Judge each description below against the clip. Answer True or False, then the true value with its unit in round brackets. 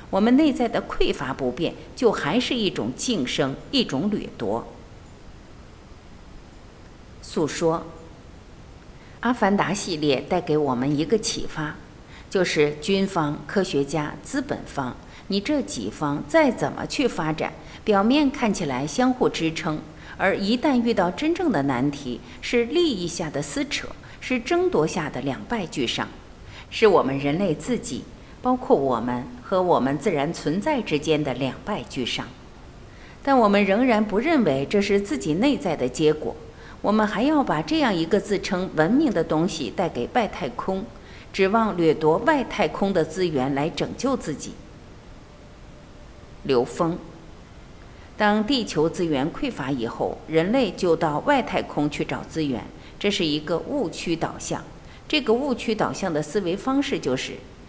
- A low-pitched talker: False (180 Hz)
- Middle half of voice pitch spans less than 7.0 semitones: False (8.4 semitones)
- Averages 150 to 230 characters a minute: True (220 characters per minute)